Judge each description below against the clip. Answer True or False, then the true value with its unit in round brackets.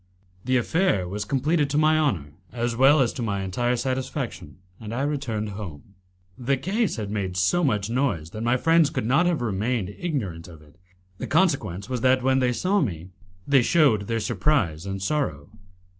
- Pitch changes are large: True (6.2 semitones)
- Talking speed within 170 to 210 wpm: True (185 wpm)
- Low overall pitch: True (120 Hz)